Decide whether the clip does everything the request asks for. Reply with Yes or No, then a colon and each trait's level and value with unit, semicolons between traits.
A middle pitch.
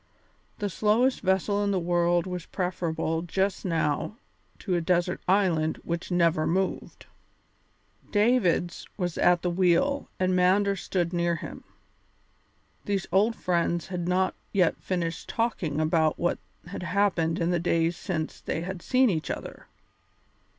Yes: medium, 180 Hz